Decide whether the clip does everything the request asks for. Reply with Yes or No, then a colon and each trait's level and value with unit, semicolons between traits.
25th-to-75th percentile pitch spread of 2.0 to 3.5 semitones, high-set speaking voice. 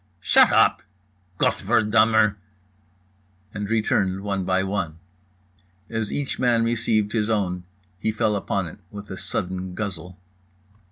No: narrow, 2.6 semitones; low, 100 Hz